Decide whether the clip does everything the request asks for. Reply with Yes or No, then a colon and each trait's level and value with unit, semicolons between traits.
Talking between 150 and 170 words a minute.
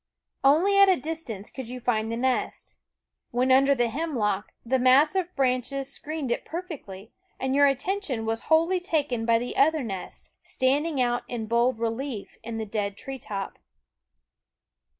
Yes: average, 160 wpm